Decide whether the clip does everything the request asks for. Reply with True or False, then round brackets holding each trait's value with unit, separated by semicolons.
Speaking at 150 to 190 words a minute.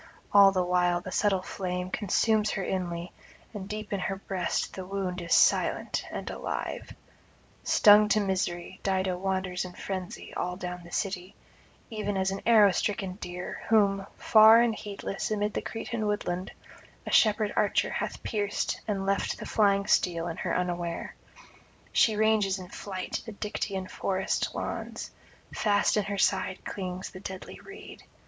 True (155 wpm)